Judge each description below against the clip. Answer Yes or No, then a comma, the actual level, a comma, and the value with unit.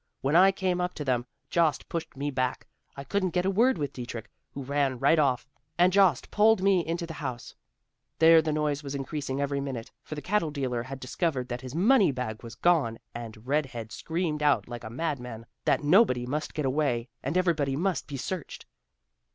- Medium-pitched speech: Yes, medium, 145 Hz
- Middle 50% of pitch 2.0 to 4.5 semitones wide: No, average, 4.9 semitones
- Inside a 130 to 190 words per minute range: No, fast, 205 wpm